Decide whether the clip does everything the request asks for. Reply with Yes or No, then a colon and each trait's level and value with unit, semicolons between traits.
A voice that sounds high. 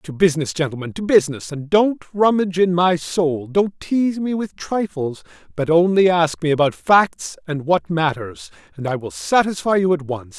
No: medium, 165 Hz